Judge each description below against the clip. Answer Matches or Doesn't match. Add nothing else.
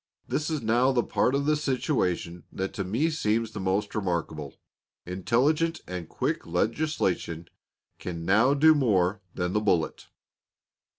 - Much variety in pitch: Matches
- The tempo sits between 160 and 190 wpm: Doesn't match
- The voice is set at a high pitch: Doesn't match